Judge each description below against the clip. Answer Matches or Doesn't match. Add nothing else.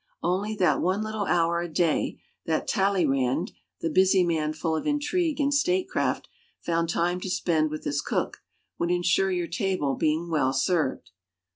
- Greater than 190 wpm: Doesn't match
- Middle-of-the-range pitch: Matches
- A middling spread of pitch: Matches